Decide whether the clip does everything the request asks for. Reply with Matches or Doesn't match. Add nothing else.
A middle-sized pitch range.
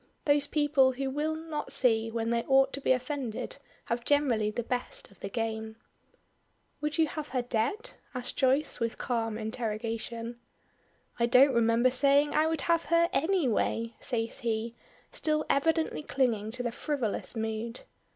Matches